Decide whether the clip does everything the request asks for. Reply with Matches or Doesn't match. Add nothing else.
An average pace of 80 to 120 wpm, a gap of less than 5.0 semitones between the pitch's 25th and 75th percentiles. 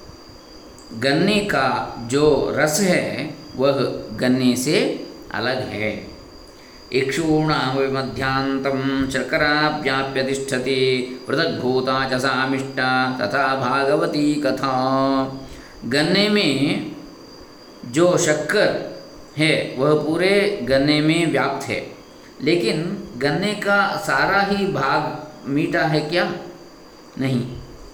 Matches